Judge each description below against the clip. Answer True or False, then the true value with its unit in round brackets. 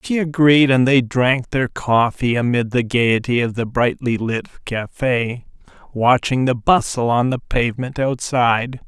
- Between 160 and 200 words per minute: False (150 wpm)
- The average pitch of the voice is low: True (125 Hz)